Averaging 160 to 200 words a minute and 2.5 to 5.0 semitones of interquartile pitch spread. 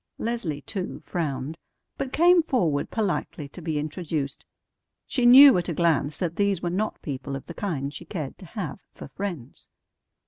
No: average, 170 wpm; wide, 5.6 semitones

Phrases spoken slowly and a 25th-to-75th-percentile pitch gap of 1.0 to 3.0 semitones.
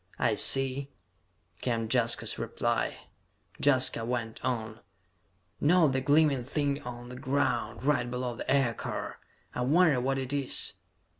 Yes: slow, 130 wpm; narrow, 2.6 semitones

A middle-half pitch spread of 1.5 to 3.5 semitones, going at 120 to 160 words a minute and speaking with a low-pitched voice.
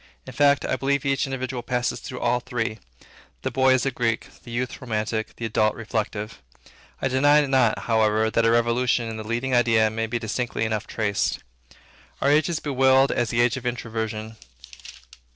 No: average, 2.8 semitones; average, 180 wpm; low, 120 Hz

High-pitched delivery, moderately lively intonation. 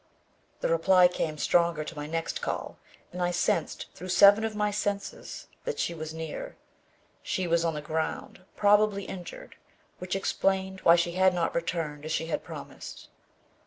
No: medium, 175 Hz; average, 3.2 semitones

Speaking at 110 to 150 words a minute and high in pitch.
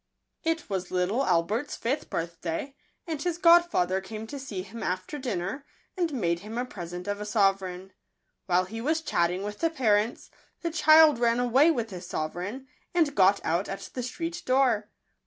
No: average, 175 wpm; high, 220 Hz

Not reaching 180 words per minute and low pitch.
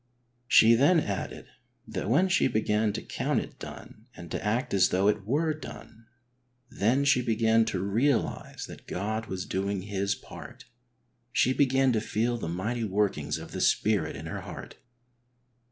Yes: average, 165 wpm; low, 110 Hz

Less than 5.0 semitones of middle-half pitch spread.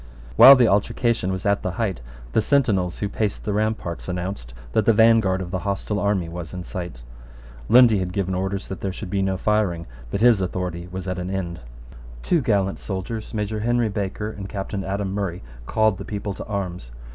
Yes: average, 2.8 semitones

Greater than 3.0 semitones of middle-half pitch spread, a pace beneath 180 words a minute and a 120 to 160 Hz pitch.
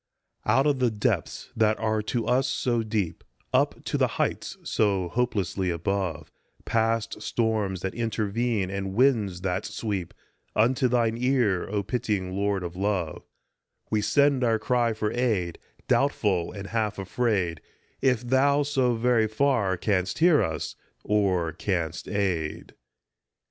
No: average, 4.2 semitones; average, 140 wpm; low, 105 Hz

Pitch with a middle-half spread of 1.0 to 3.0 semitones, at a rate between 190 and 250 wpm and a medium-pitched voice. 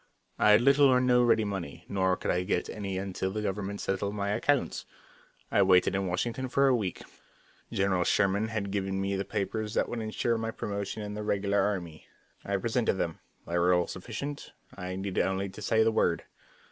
No: average, 2.7 semitones; average, 195 wpm; low, 100 Hz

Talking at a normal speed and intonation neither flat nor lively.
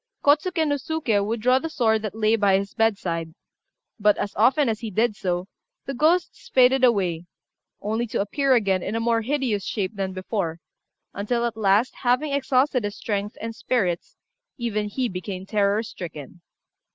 Yes: average, 170 wpm; average, 4.1 semitones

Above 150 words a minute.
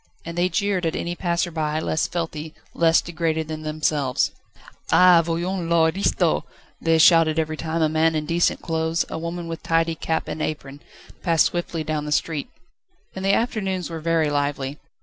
Yes: average, 170 wpm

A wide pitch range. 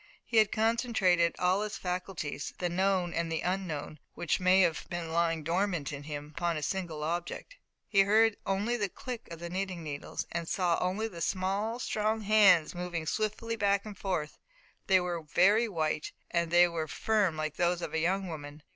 No: average, 3.4 semitones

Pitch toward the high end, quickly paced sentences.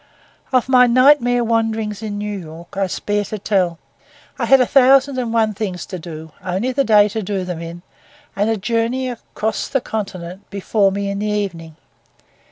No: high, 210 Hz; average, 180 wpm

